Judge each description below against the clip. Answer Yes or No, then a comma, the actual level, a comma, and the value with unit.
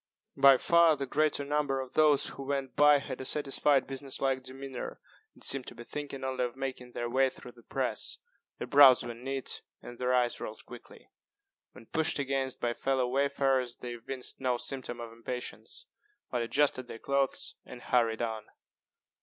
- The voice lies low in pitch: Yes, low, 130 Hz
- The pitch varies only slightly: Yes, narrow, 2.0 semitones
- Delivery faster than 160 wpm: Yes, average, 180 wpm